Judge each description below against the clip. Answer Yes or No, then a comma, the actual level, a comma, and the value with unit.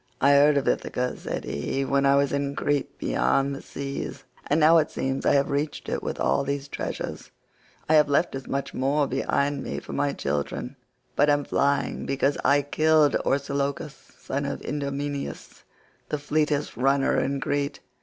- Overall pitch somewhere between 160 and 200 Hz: No, medium, 140 Hz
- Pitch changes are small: Yes, narrow, 0.9 semitones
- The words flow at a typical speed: Yes, average, 175 wpm